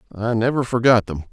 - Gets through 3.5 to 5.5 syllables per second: No, 6.1 syllables/s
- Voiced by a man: Yes, male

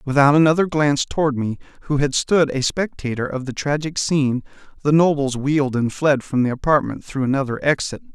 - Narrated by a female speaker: No, male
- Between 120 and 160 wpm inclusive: No, average, 185 wpm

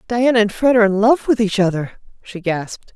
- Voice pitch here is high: Yes, high, 210 Hz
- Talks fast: Yes, fast, 225 wpm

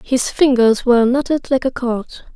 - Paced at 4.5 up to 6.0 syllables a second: Yes, 5.0 syllables/s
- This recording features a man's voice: No, female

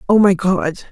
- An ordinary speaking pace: Yes, average, 195 wpm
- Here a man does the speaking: No, female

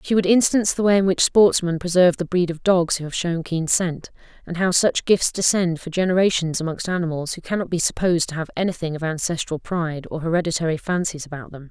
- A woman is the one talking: Yes, female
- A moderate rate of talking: No, fast, 215 wpm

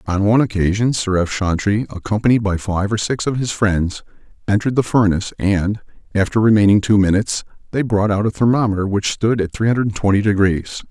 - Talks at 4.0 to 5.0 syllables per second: No, 5.9 syllables/s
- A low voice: Yes, low, 105 Hz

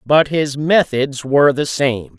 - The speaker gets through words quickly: No, average, 165 wpm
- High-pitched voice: No, medium, 140 Hz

